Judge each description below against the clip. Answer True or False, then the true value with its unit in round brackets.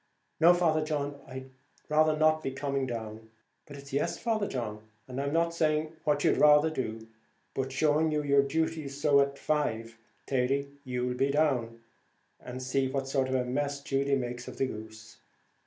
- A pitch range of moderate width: True (3.1 semitones)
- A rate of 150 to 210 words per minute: True (175 wpm)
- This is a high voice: False (140 Hz)